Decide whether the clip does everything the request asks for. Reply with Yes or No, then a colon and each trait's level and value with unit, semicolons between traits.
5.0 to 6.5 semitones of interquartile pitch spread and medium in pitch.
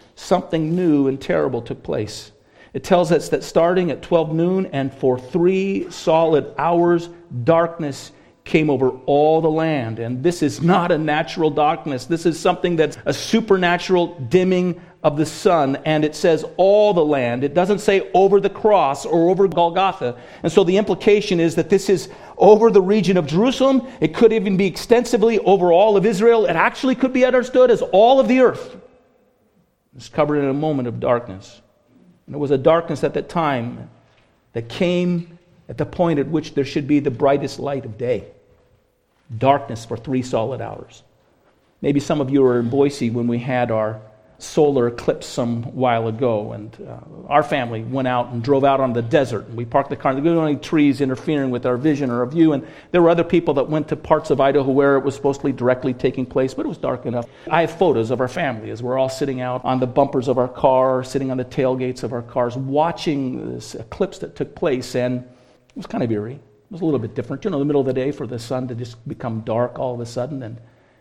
Yes: wide, 5.4 semitones; medium, 145 Hz